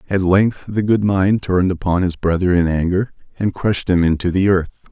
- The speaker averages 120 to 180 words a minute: No, fast, 205 wpm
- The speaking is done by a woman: No, male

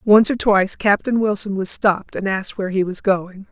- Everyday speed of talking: No, fast, 220 wpm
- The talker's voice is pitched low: No, high, 200 Hz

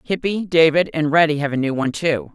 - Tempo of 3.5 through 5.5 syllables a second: No, 5.8 syllables/s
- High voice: No, medium, 160 Hz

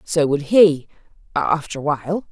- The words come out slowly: Yes, slow, 130 wpm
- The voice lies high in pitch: No, medium, 160 Hz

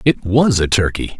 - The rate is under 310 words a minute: Yes, average, 200 wpm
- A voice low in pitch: Yes, low, 110 Hz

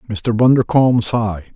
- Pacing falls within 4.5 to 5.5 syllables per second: No, 5.7 syllables/s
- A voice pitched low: Yes, low, 115 Hz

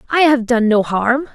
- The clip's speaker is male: No, female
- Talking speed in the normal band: No, fast, 220 wpm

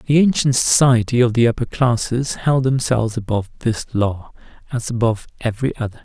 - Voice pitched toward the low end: Yes, low, 120 Hz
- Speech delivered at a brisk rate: No, average, 160 wpm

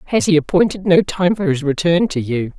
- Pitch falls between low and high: Yes, medium, 170 Hz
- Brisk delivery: Yes, fast, 230 wpm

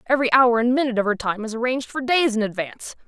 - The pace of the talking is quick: Yes, fast, 255 wpm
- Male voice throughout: No, female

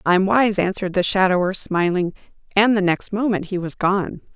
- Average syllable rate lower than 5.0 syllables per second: No, 5.1 syllables/s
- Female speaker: Yes, female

